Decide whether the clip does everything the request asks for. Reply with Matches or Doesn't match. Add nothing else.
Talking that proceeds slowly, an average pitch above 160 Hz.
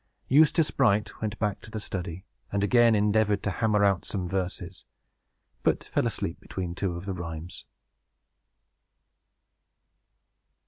Doesn't match